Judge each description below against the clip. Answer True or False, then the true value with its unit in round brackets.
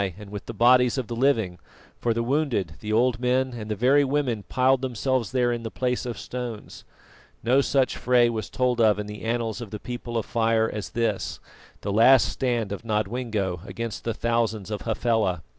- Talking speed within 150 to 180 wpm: False (195 wpm)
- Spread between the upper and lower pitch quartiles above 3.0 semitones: False (2.7 semitones)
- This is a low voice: True (115 Hz)